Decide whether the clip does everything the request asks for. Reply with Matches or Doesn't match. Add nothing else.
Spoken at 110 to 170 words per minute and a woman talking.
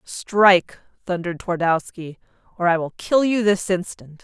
Matches